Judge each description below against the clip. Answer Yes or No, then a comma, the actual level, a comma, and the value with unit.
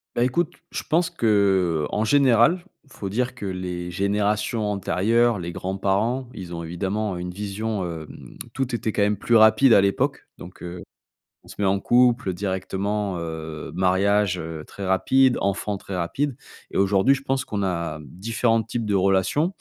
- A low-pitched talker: Yes, low, 100 Hz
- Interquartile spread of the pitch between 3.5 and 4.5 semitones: Yes, average, 3.9 semitones